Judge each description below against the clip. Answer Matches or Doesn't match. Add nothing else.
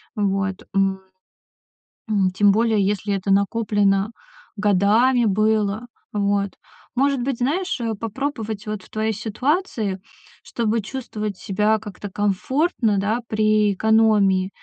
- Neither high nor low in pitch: Doesn't match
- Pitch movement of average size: Doesn't match